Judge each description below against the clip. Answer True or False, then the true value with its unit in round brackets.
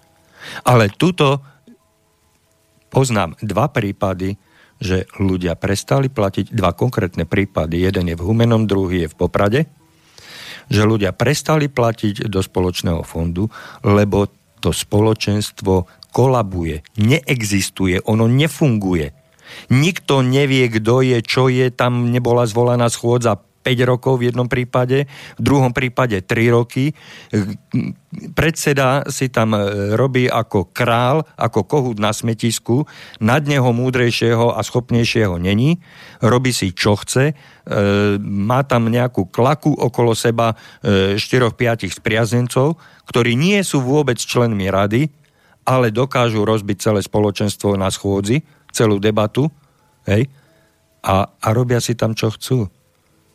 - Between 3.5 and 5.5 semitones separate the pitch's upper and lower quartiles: True (4.3 semitones)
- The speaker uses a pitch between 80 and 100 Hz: False (115 Hz)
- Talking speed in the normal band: True (120 wpm)